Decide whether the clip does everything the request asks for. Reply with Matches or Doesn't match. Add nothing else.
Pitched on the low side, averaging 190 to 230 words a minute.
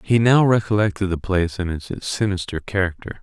Doesn't match